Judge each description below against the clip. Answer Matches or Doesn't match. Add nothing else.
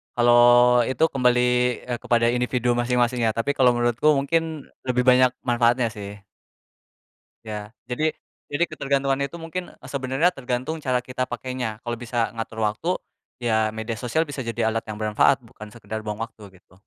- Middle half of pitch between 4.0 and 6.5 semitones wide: Doesn't match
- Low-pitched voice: Matches